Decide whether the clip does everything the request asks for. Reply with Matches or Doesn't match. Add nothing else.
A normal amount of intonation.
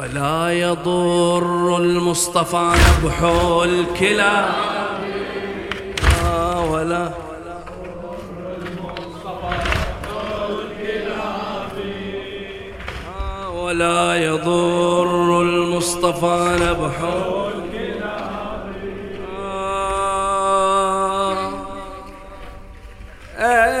Doesn't match